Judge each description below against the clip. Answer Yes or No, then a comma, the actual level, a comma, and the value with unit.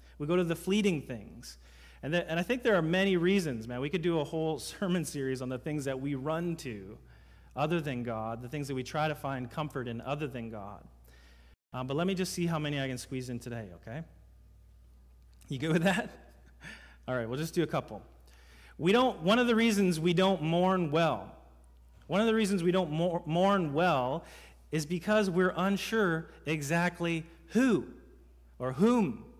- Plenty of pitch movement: Yes, wide, 7.4 semitones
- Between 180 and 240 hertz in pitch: No, medium, 155 Hz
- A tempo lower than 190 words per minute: No, average, 200 wpm